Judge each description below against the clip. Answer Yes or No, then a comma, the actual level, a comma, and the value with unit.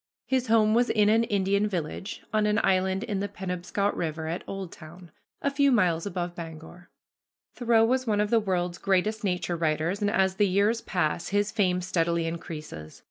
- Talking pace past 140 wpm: Yes, average, 180 wpm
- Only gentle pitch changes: No, average, 3.5 semitones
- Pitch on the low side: No, high, 190 Hz